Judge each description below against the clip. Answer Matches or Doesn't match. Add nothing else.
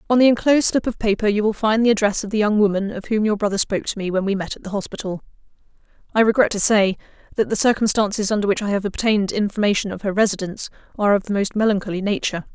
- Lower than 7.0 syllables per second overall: Doesn't match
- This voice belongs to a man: Doesn't match